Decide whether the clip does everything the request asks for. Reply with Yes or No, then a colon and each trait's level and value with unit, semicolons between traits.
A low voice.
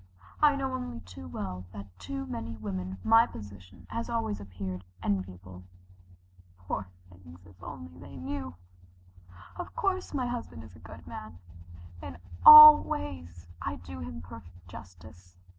Yes: very low, 95 Hz